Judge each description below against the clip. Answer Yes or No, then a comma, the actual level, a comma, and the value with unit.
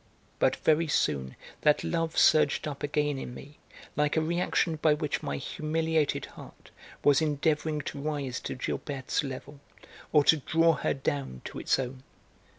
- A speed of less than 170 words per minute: Yes, average, 155 wpm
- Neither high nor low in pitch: Yes, medium, 150 Hz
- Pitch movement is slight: Yes, narrow, 2.3 semitones